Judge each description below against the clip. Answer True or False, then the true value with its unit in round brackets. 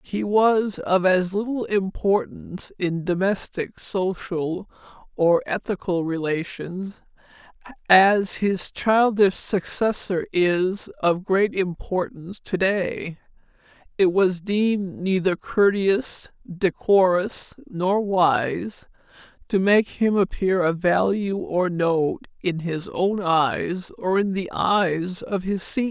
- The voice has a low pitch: False (190 Hz)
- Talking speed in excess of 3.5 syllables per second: False (3.3 syllables/s)